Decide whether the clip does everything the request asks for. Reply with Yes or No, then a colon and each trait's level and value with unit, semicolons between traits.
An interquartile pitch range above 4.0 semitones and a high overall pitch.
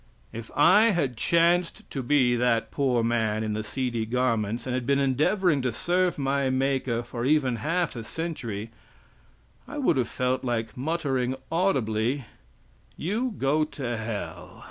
No: average, 4.5 semitones; low, 130 Hz